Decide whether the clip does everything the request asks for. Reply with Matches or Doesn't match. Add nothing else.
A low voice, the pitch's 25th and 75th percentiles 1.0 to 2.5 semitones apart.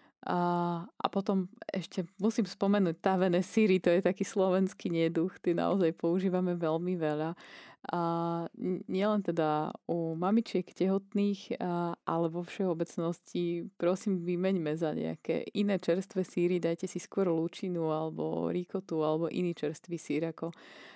Doesn't match